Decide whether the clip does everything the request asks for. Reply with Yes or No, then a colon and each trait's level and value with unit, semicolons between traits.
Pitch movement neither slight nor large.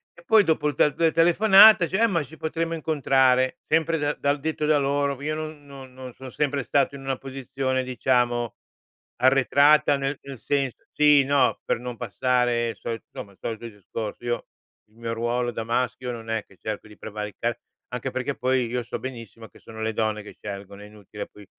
Yes: average, 3.9 semitones